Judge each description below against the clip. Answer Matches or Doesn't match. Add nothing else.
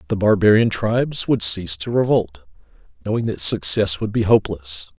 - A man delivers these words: Matches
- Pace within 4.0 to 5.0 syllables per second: Doesn't match